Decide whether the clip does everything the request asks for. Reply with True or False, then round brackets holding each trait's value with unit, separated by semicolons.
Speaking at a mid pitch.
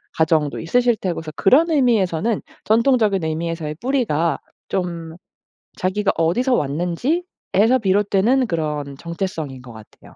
True (180 Hz)